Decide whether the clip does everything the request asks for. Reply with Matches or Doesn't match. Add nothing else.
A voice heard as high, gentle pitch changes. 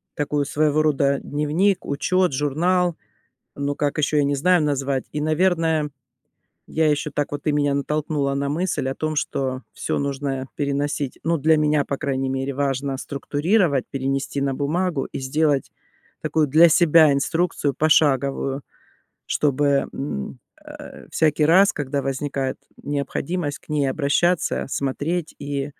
Doesn't match